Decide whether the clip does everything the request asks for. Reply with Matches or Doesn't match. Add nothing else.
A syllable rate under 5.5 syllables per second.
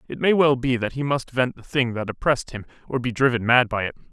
Doesn't match